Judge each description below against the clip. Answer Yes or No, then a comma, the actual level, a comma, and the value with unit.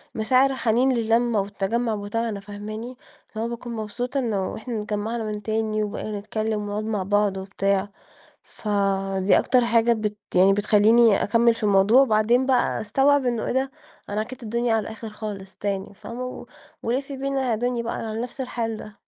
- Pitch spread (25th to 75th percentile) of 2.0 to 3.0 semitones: Yes, narrow, 2.5 semitones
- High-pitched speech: Yes, high, 220 Hz